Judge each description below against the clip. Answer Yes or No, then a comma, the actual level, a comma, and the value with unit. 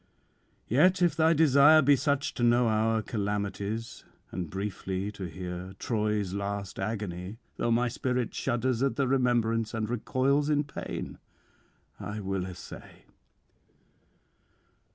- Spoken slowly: Yes, slow, 125 wpm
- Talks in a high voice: No, low, 115 Hz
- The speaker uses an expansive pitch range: No, average, 4.5 semitones